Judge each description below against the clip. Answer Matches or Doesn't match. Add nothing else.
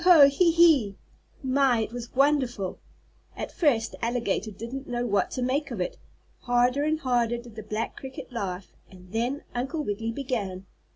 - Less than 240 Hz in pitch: Doesn't match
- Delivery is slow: Doesn't match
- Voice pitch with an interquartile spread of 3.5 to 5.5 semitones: Matches